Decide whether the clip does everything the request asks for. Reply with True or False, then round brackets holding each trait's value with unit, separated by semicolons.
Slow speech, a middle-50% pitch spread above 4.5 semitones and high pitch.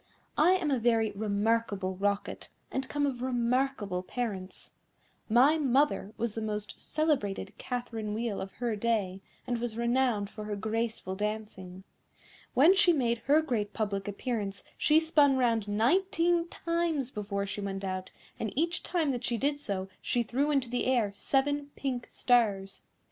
False (155 wpm; 5.0 semitones; 235 Hz)